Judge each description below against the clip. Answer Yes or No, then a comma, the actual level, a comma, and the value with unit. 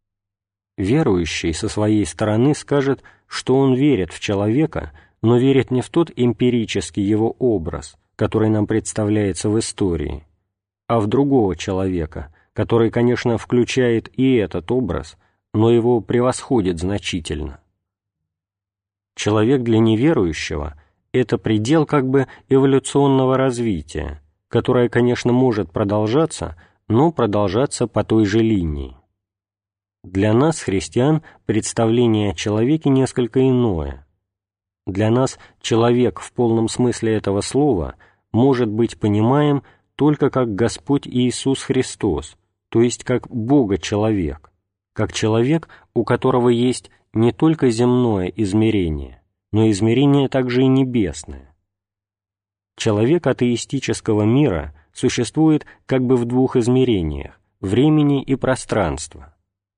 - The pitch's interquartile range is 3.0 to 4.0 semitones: No, average, 4.4 semitones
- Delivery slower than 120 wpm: Yes, slow, 110 wpm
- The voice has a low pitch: Yes, low, 110 Hz